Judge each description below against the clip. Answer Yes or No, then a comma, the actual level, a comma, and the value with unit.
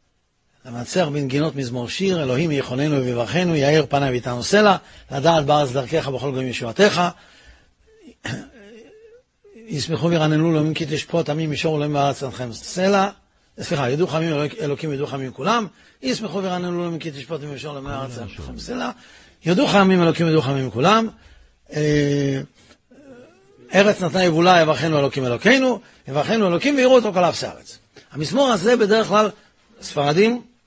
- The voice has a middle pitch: Yes, medium, 155 Hz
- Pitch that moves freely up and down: Yes, wide, 5.7 semitones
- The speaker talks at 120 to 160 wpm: Yes, average, 135 wpm